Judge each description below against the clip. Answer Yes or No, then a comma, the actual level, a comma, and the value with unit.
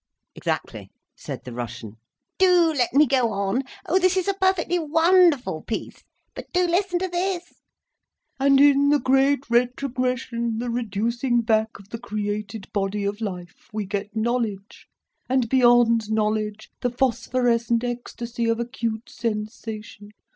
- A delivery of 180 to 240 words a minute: No, average, 140 wpm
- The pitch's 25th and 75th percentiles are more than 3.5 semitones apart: Yes, average, 4.5 semitones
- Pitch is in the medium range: No, high, 235 Hz